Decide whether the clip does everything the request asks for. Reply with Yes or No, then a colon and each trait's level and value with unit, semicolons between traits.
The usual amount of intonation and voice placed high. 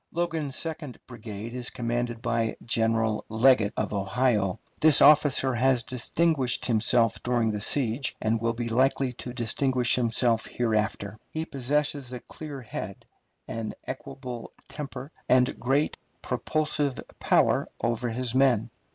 No: average, 3.0 semitones; low, 125 Hz